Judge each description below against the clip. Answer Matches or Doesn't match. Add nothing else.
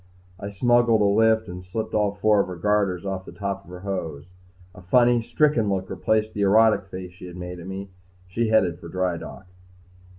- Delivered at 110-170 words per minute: Doesn't match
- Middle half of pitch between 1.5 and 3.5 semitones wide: Matches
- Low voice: Matches